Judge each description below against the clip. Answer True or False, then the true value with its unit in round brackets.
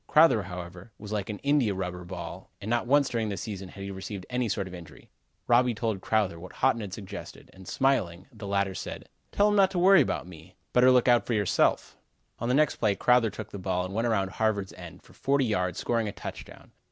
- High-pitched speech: False (105 Hz)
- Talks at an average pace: False (225 wpm)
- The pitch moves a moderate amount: True (4.5 semitones)